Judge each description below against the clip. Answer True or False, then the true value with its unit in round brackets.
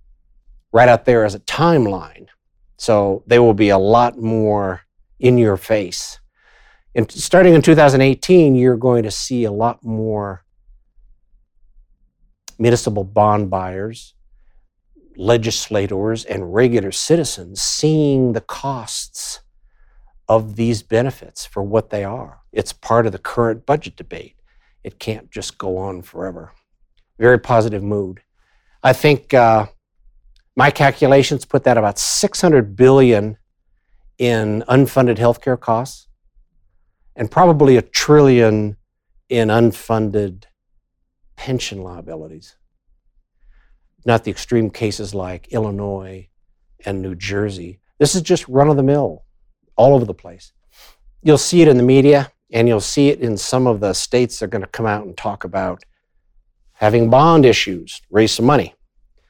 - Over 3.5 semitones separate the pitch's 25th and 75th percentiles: True (4.5 semitones)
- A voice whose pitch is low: True (115 Hz)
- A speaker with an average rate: False (130 wpm)